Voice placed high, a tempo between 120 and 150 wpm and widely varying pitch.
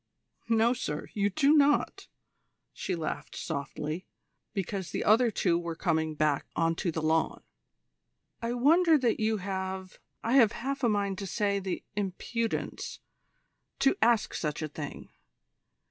Yes: high, 200 Hz; average, 145 wpm; wide, 5.7 semitones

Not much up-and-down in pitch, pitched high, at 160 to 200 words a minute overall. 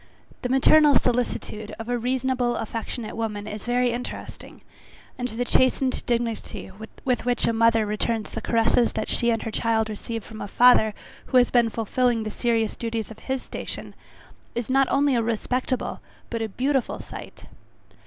Yes: narrow, 2.0 semitones; high, 235 Hz; average, 165 wpm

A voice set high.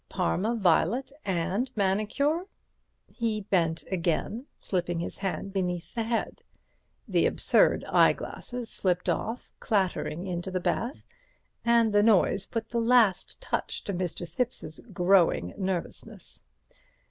Yes: high, 195 Hz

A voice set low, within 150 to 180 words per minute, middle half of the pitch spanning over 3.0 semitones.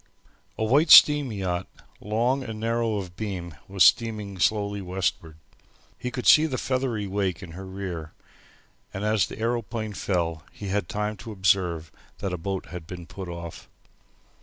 Yes: low, 100 Hz; average, 160 wpm; average, 3.7 semitones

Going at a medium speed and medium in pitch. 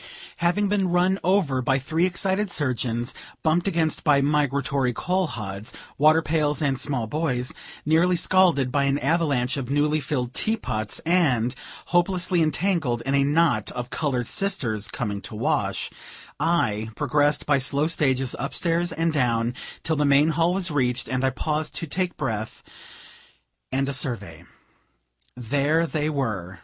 Yes: average, 155 wpm; medium, 145 Hz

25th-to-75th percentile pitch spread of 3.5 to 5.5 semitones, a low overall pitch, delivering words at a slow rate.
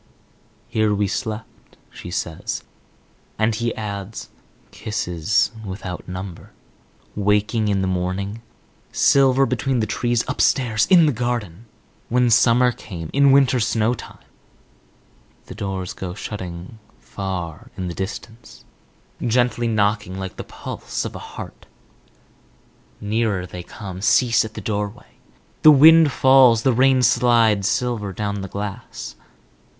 Yes: average, 3.9 semitones; low, 110 Hz; slow, 125 wpm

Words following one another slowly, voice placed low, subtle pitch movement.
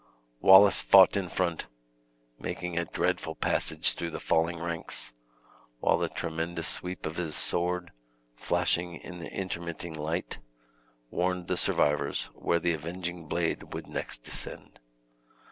Yes: slow, 130 wpm; very low, 85 Hz; narrow, 1.4 semitones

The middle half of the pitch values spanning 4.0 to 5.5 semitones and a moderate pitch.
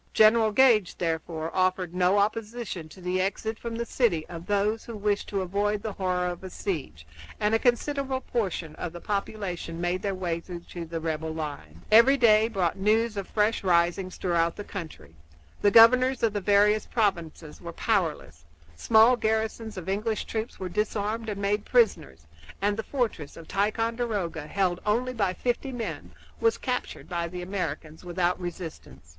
No: average, 4.3 semitones; high, 200 Hz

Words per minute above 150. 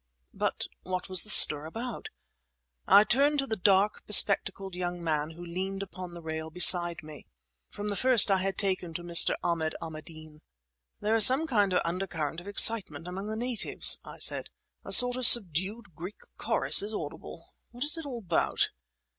Yes: average, 175 wpm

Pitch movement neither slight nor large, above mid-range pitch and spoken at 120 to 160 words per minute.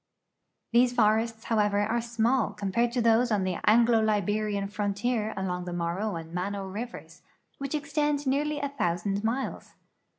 Yes: average, 3.3 semitones; high, 220 Hz; average, 145 wpm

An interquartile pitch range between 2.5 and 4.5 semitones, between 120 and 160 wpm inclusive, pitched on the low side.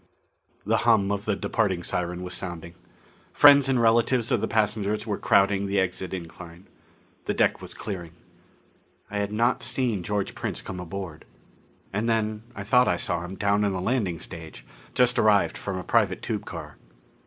No: average, 3.4 semitones; average, 175 wpm; low, 100 Hz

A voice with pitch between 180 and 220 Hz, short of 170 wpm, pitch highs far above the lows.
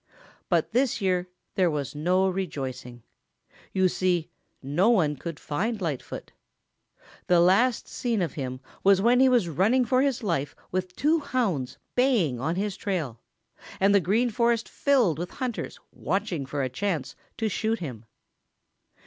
Yes: medium, 185 Hz; average, 150 wpm; wide, 7.2 semitones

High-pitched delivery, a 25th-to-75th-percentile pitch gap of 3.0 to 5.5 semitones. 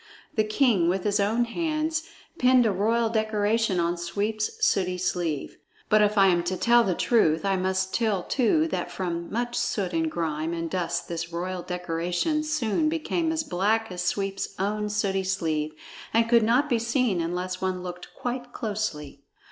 Yes: high, 195 Hz; average, 4.6 semitones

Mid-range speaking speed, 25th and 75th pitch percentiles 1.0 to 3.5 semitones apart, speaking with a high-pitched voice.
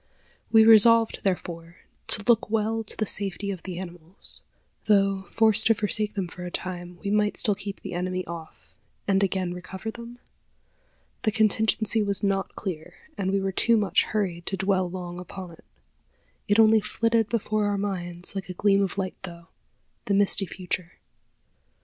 Yes: average, 170 wpm; average, 2.9 semitones; high, 195 Hz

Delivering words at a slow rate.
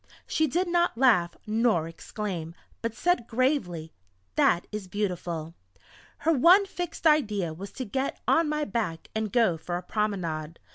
No: average, 150 wpm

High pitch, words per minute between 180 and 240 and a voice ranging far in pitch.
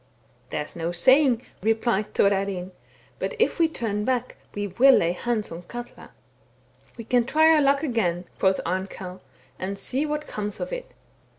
Yes: high, 220 Hz; average, 185 wpm; wide, 6.0 semitones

